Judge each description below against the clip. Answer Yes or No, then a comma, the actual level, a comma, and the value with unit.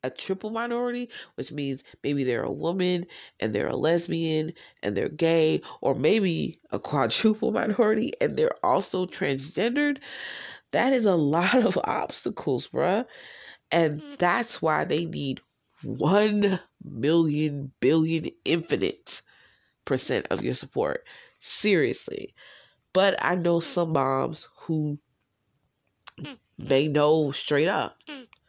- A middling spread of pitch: No, wide, 6.5 semitones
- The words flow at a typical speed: No, slow, 120 wpm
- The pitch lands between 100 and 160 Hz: No, medium, 170 Hz